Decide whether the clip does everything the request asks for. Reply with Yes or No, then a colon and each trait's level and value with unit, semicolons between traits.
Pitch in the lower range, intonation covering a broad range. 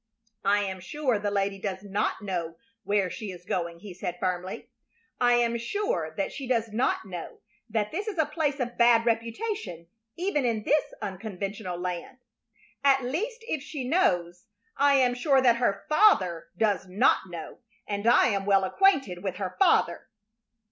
No: high, 220 Hz; wide, 6.2 semitones